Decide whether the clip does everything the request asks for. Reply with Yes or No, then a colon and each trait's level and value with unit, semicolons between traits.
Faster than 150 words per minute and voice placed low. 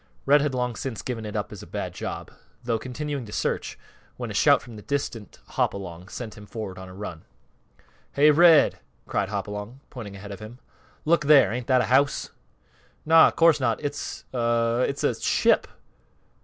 Yes: average, 185 wpm; low, 120 Hz